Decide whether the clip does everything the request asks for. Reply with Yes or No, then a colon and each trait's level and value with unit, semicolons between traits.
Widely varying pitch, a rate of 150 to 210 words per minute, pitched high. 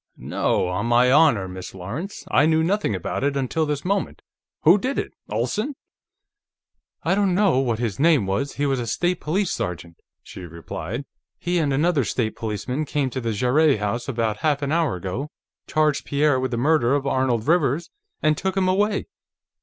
No: wide, 5.8 semitones; average, 185 wpm; medium, 140 Hz